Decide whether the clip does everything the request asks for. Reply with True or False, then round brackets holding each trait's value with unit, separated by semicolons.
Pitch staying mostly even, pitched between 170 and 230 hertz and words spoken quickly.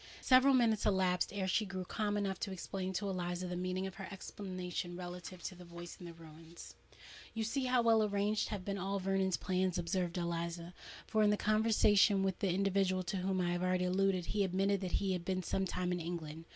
True (2.1 semitones; 185 Hz; 215 wpm)